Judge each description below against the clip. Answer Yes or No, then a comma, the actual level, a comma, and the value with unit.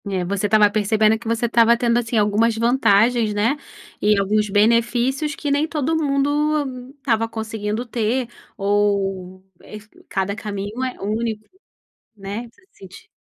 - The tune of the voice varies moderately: Yes, average, 3.2 semitones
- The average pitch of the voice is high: Yes, high, 225 Hz